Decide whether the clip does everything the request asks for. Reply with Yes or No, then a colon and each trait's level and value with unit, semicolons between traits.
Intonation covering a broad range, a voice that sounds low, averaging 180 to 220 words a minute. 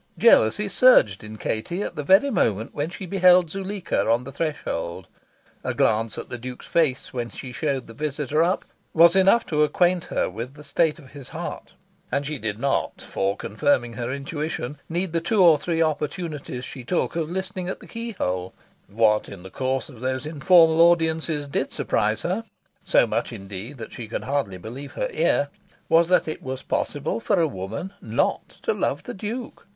No: wide, 6.4 semitones; medium, 145 Hz; average, 190 wpm